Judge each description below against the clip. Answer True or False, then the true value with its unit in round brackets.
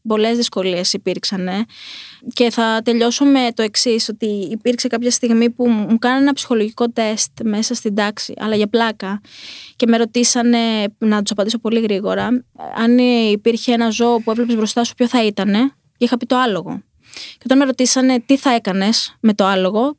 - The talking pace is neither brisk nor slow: False (175 wpm)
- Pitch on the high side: True (230 Hz)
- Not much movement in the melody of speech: True (2.1 semitones)